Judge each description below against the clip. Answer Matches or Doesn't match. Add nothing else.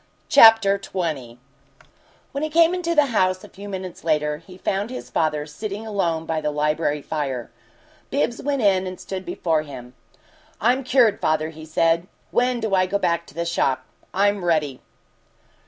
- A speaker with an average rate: Matches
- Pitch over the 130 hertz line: Matches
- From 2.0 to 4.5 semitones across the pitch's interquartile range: Doesn't match